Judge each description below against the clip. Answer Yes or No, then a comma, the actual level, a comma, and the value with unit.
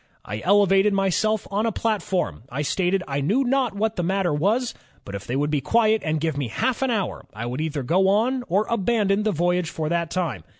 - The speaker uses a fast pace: Yes, fast, 225 wpm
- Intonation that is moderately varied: No, wide, 5.8 semitones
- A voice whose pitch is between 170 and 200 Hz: Yes, high, 190 Hz